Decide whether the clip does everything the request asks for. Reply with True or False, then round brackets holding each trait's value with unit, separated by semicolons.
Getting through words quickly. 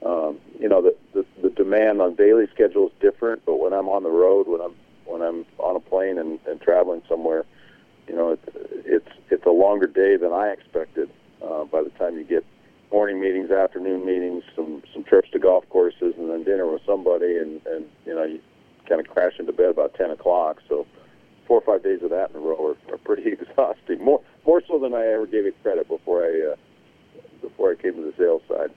True (225 wpm)